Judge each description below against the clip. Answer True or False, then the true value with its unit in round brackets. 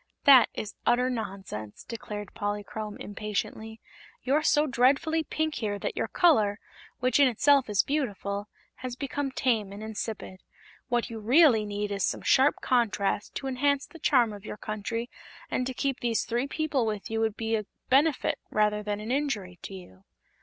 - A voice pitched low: False (225 Hz)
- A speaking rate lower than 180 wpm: True (170 wpm)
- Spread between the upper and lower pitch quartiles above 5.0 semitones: False (4.3 semitones)